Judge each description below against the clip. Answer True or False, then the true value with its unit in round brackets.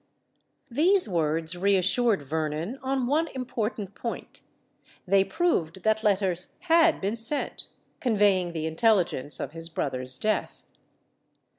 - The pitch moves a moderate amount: False (6.7 semitones)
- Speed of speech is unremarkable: False (115 wpm)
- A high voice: True (200 Hz)